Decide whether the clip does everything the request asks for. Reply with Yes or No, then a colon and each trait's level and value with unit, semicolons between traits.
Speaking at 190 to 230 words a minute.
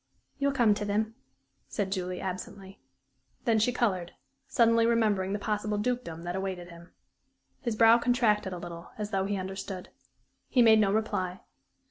No: average, 155 wpm